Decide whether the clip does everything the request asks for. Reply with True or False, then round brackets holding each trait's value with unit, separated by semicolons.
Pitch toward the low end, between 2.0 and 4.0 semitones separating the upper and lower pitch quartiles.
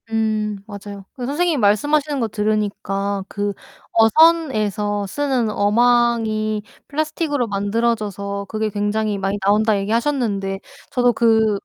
False (215 Hz; 2.9 semitones)